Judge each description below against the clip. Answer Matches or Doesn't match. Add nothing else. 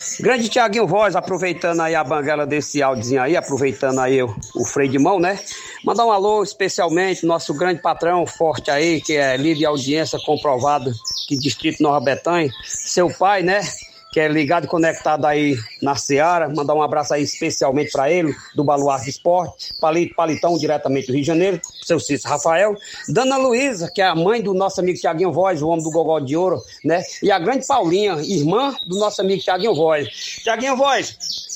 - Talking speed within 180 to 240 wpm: Matches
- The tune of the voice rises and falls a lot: Doesn't match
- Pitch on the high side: Doesn't match